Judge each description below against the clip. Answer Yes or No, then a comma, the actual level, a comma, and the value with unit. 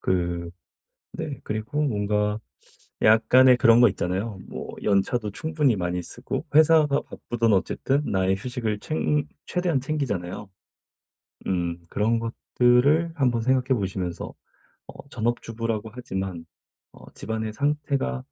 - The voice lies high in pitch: No, low, 115 Hz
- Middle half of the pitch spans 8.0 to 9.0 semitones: No, average, 5.3 semitones